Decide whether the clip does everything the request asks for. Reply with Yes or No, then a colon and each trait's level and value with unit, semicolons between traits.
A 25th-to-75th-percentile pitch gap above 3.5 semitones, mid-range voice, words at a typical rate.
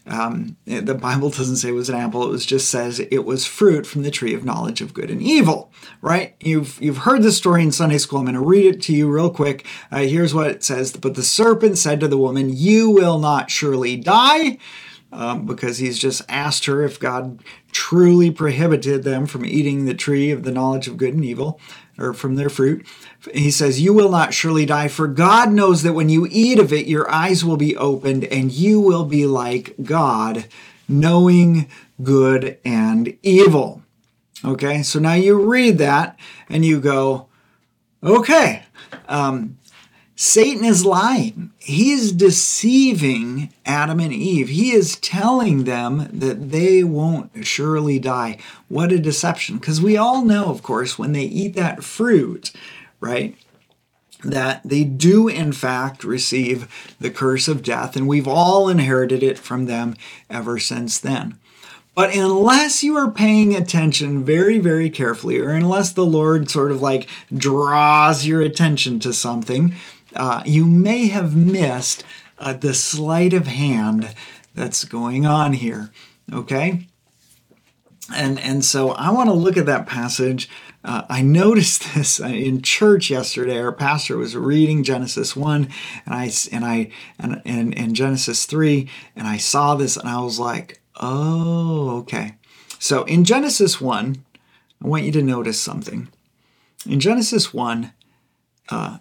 Yes: average, 5.2 semitones; medium, 145 Hz; average, 165 wpm